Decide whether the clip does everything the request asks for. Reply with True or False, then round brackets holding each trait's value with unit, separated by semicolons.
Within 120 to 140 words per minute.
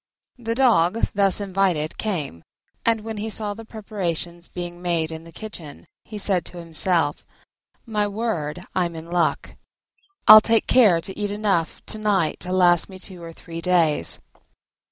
False (160 wpm)